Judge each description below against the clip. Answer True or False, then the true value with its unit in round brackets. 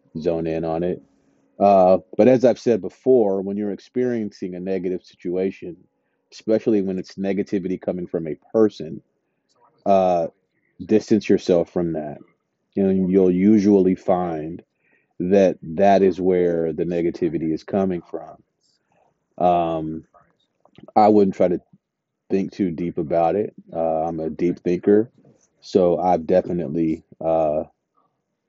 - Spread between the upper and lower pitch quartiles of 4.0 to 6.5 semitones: False (2.9 semitones)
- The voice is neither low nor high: False (95 Hz)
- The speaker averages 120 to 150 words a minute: True (135 wpm)